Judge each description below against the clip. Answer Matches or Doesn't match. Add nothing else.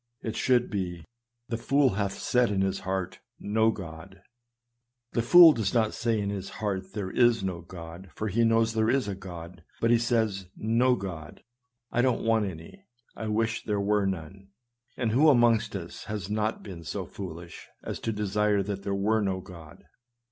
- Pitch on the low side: Matches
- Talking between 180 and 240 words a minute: Matches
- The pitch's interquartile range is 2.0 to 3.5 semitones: Matches